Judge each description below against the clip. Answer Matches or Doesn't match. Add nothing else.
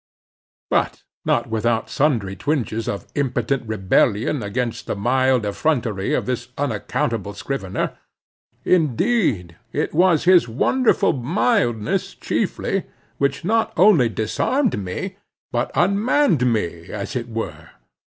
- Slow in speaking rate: Matches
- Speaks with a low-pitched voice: Matches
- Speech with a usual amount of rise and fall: Doesn't match